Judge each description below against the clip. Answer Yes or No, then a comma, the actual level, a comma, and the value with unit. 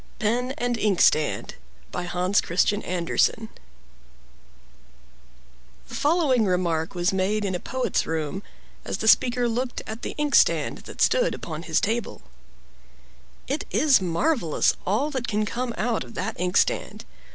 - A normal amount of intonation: No, wide, 5.7 semitones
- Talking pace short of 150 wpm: Yes, average, 140 wpm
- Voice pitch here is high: Yes, high, 215 Hz